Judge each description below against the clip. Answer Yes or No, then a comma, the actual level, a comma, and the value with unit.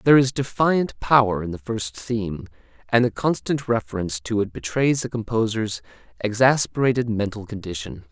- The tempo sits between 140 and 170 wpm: Yes, average, 150 wpm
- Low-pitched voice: Yes, low, 110 Hz